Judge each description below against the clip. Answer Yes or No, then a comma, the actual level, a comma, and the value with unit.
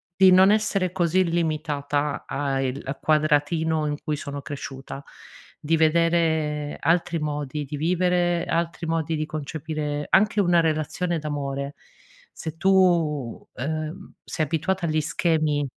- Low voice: No, medium, 155 Hz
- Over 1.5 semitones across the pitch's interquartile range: Yes, narrow, 2.5 semitones